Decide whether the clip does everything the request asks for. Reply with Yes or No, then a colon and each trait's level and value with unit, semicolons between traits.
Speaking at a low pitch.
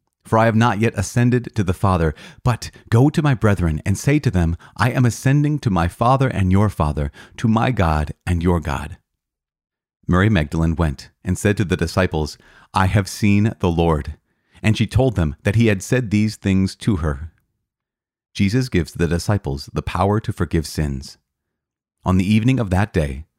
Yes: very low, 95 Hz